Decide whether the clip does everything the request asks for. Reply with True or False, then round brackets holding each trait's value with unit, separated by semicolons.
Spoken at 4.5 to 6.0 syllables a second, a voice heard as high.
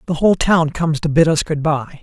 False (5.9 syllables/s; 155 Hz)